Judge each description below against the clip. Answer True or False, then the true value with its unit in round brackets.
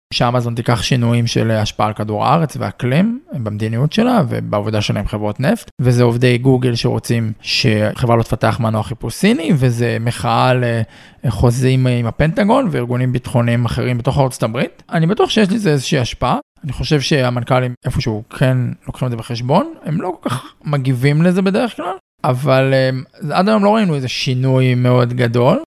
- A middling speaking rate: False (165 wpm)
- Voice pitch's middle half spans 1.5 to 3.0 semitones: False (4.2 semitones)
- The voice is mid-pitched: False (125 Hz)